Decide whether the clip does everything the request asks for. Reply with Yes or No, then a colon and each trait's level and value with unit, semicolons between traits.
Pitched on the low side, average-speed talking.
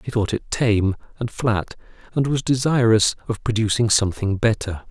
Yes: low, 110 Hz; average, 160 wpm